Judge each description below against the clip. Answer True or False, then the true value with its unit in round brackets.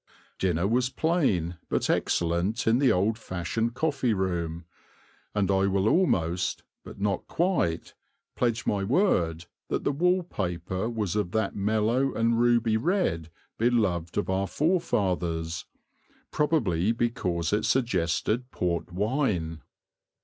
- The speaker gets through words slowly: True (125 wpm)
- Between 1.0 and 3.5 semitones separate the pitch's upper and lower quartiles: False (5.6 semitones)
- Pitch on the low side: True (105 Hz)